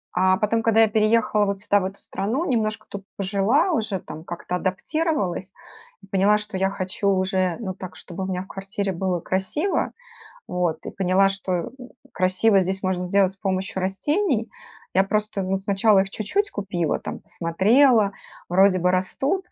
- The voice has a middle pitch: No, high, 195 Hz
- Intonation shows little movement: Yes, narrow, 2.3 semitones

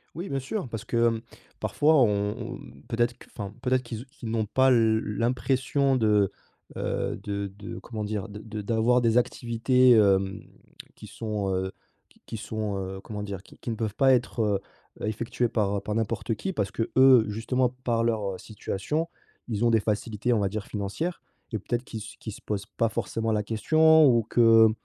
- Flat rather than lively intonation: No, average, 3.0 semitones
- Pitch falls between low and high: No, low, 115 Hz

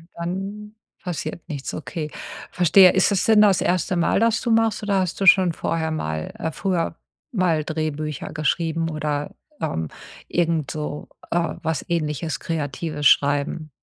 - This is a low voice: No, medium, 165 Hz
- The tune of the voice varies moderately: Yes, average, 3.4 semitones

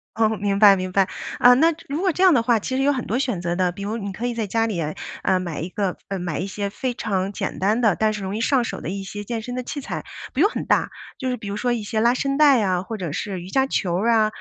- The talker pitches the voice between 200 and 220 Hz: Yes, high, 215 Hz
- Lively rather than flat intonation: No, average, 4.4 semitones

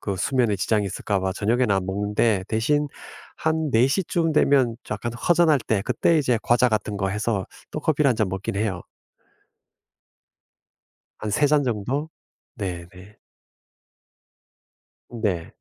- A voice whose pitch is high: No, low, 110 Hz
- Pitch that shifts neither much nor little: No, wide, 5.8 semitones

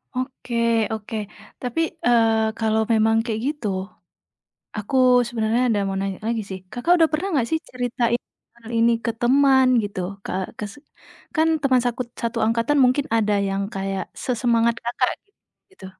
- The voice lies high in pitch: Yes, high, 235 Hz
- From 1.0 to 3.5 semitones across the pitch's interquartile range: Yes, narrow, 2.6 semitones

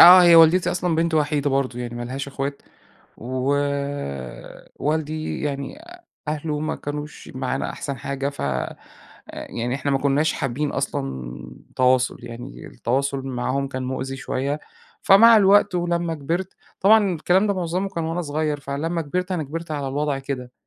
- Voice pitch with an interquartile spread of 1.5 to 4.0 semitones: Yes, average, 3.7 semitones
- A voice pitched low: No, medium, 145 Hz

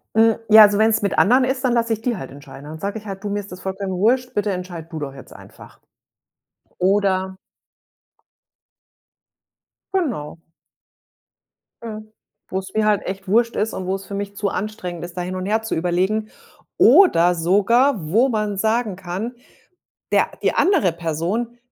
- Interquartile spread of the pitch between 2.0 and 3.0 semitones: No, average, 3.4 semitones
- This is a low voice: No, high, 200 Hz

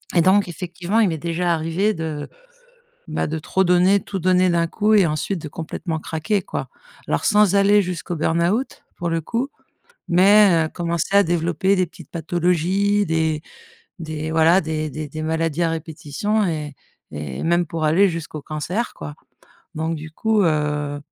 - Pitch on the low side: No, medium, 170 Hz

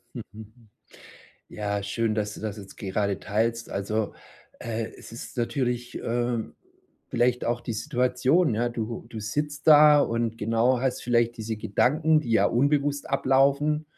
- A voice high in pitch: No, low, 120 Hz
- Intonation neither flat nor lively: Yes, average, 3.5 semitones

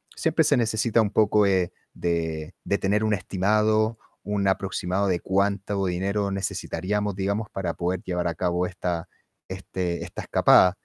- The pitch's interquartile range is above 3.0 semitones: No, narrow, 2.6 semitones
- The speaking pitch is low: Yes, very low, 95 Hz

